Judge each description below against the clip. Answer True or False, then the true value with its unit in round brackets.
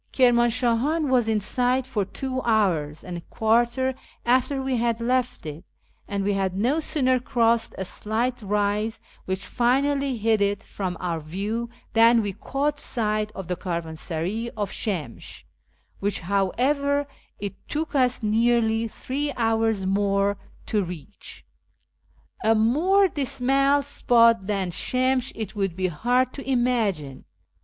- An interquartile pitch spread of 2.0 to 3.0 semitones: False (4.4 semitones)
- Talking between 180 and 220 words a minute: False (140 wpm)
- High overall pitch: True (225 Hz)